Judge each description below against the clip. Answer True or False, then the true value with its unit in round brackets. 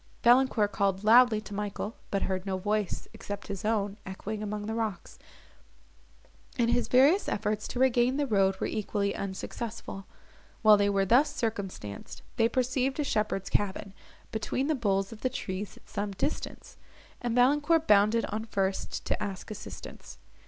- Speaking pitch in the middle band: False (210 Hz)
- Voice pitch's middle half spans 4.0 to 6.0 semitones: False (3.4 semitones)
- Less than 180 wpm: True (160 wpm)